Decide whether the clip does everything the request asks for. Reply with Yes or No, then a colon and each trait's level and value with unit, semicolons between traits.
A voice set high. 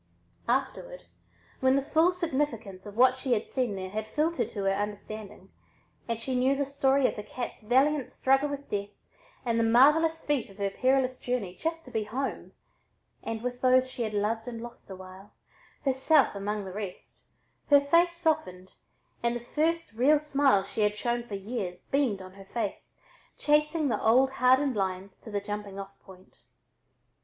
Yes: high, 240 Hz